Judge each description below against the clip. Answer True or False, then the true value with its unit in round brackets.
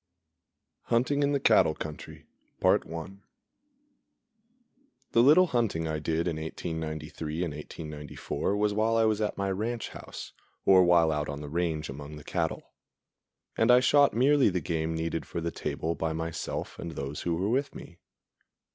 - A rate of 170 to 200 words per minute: False (160 wpm)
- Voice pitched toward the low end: True (85 Hz)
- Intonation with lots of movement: True (7.1 semitones)